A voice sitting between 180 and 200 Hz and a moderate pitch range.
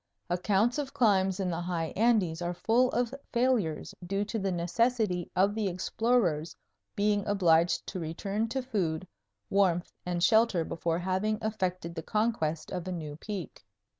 Yes: high, 190 Hz; average, 4.1 semitones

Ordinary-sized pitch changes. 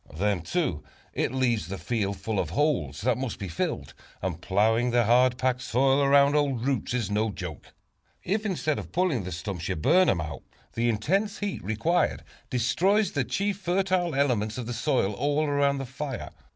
No: wide, 5.9 semitones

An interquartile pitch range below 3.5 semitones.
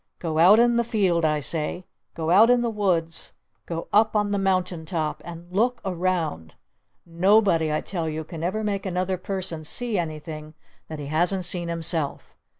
No: average, 3.8 semitones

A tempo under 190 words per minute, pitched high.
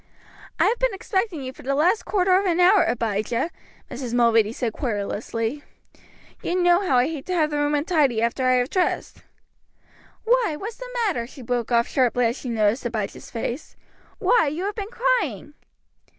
Yes: average, 180 wpm; very high, 280 Hz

